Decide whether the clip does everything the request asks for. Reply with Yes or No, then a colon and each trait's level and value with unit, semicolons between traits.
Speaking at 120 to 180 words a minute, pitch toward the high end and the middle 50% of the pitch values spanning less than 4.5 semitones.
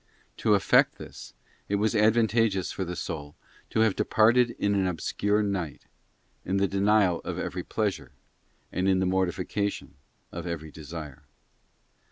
No: average, 145 wpm; very low, 95 Hz; average, 3.5 semitones